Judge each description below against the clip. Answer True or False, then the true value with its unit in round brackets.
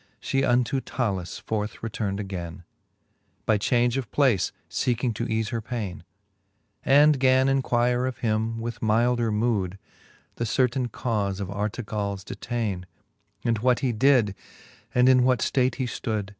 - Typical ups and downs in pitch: True (3.3 semitones)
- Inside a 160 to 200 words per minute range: False (145 wpm)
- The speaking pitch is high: False (115 Hz)